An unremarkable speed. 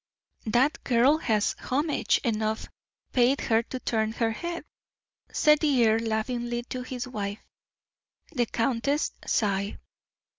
No: slow, 120 wpm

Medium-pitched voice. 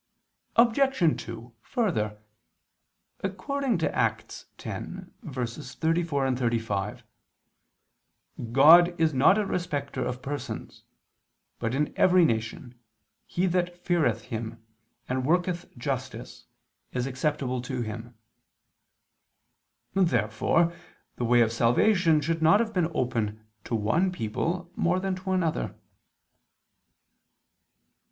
Yes: medium, 145 Hz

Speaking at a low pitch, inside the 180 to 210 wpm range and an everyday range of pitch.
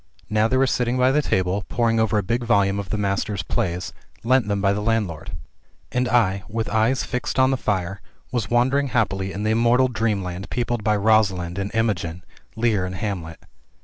Yes: low, 110 Hz; average, 190 wpm; average, 3.5 semitones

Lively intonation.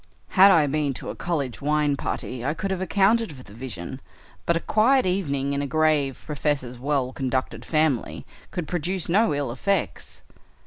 No: average, 4.8 semitones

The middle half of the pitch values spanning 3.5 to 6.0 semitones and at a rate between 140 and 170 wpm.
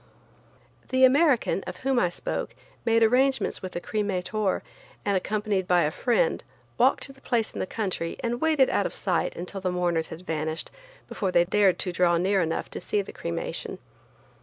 No: average, 4.7 semitones; average, 185 wpm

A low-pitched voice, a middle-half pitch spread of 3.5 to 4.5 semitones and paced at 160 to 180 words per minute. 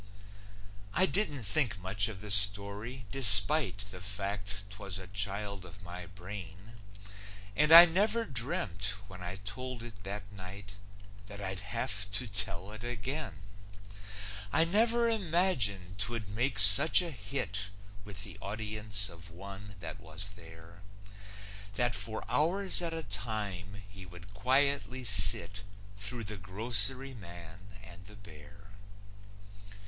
No: low, 100 Hz; average, 4.1 semitones; slow, 135 wpm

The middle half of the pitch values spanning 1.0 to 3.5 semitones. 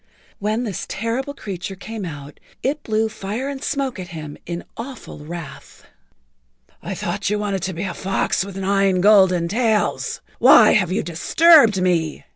No: average, 4.3 semitones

